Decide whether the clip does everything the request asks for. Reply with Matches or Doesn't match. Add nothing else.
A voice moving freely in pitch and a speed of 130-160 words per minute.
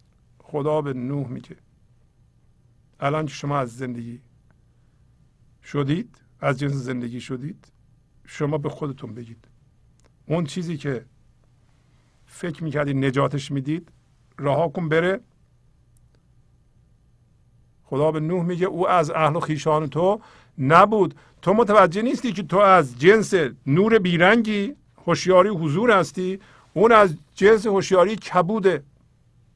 Doesn't match